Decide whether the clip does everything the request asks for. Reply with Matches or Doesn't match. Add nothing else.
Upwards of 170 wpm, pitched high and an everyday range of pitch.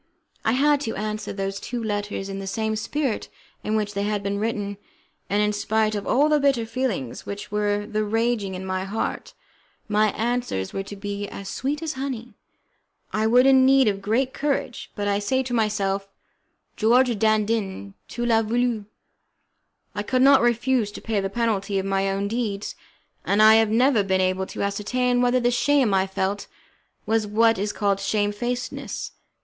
Matches